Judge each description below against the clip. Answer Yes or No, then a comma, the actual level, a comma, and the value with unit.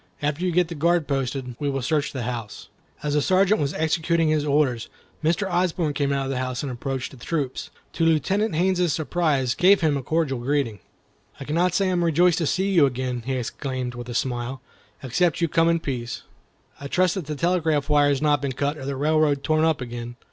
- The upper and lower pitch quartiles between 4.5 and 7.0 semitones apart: No, average, 4.1 semitones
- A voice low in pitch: No, medium, 145 Hz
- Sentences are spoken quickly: Yes, fast, 220 wpm